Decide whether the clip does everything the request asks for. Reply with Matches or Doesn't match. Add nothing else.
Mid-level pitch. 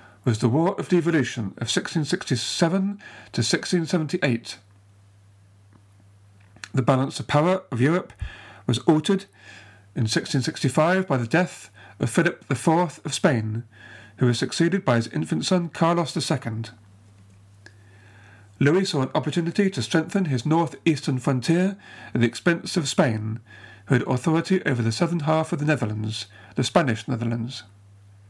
Doesn't match